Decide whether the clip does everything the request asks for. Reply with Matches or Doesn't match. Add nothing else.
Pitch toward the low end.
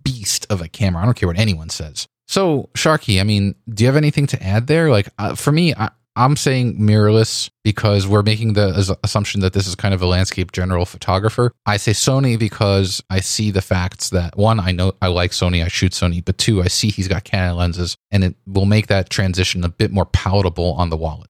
Matches